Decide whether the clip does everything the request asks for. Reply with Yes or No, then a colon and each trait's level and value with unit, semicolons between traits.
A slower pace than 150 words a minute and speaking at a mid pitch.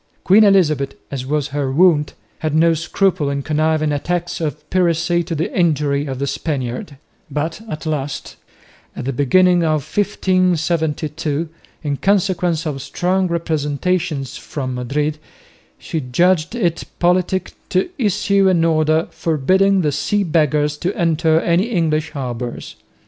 Yes: average, 140 wpm; medium, 160 Hz